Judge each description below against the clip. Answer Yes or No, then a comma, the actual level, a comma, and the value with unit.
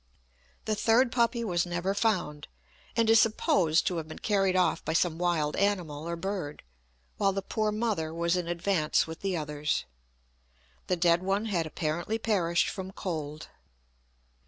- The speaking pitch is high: No, medium, 180 Hz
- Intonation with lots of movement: No, average, 3.9 semitones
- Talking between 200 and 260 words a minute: No, average, 160 wpm